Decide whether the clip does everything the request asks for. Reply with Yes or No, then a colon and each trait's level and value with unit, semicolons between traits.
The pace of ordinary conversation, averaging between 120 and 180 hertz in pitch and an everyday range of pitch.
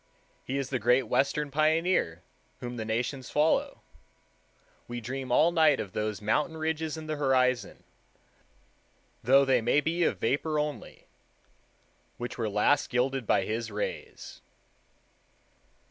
No: slow, 130 wpm; low, 135 Hz; average, 4.2 semitones